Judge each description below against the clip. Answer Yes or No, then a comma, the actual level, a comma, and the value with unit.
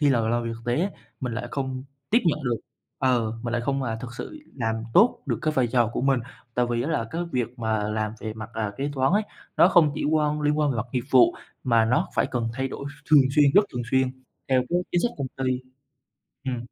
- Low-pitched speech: Yes, low, 130 Hz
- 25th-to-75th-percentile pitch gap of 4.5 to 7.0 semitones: No, average, 3.8 semitones